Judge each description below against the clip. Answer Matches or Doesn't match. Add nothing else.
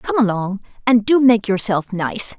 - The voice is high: Matches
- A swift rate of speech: Doesn't match